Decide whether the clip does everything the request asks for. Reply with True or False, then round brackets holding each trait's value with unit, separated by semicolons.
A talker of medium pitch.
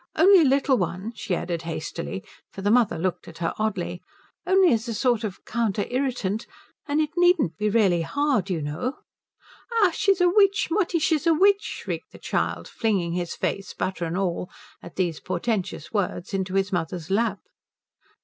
False (210 Hz)